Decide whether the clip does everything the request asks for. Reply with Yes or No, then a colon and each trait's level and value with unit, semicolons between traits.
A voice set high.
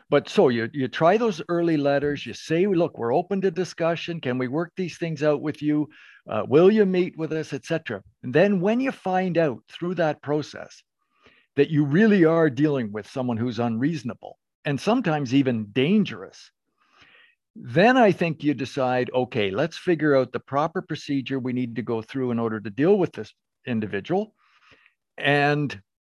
No: medium, 150 Hz